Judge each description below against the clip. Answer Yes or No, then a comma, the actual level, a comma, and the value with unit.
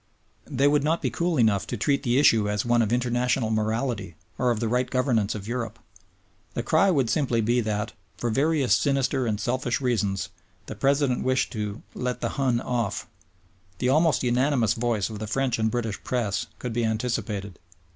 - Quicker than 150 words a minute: Yes, average, 185 wpm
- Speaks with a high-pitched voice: No, low, 120 Hz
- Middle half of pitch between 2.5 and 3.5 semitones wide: Yes, average, 3.0 semitones